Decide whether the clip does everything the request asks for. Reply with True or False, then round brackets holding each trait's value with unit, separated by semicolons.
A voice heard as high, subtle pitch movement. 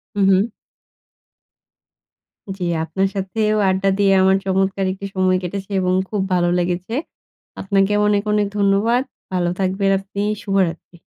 True (195 Hz; 1.3 semitones)